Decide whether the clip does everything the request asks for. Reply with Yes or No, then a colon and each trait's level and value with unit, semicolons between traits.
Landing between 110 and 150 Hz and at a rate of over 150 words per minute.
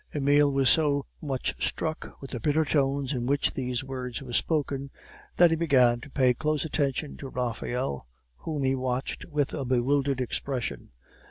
Yes: low, 135 Hz; average, 165 wpm